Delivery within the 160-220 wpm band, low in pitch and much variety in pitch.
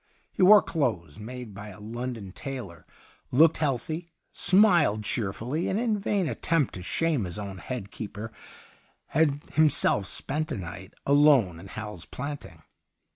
No: average, 145 wpm; low, 125 Hz; wide, 7.7 semitones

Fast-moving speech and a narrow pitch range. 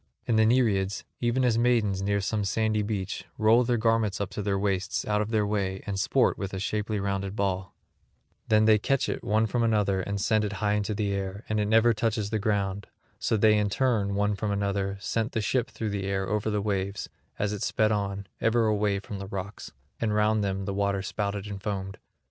Yes: fast, 220 wpm; narrow, 1.8 semitones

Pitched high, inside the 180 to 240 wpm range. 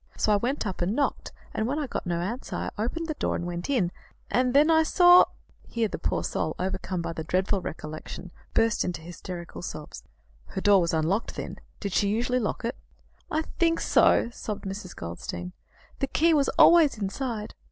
Yes: high, 210 Hz; average, 195 wpm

